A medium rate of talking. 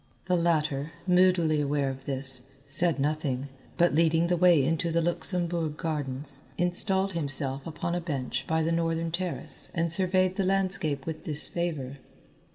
Yes: average, 150 wpm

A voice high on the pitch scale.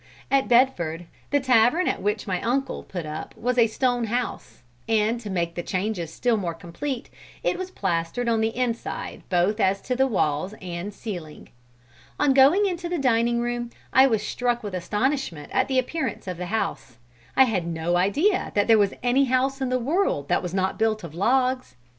Yes: high, 225 Hz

